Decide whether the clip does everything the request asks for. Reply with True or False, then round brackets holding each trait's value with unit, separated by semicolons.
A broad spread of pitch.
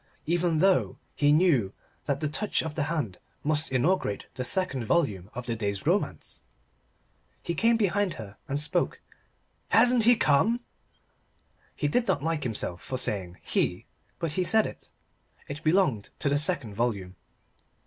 True (7.3 semitones)